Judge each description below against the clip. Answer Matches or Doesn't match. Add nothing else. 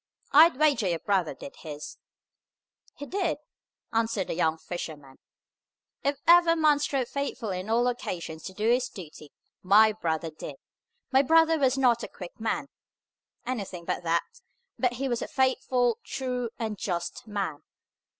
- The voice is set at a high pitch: Matches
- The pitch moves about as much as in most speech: Doesn't match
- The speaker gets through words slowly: Doesn't match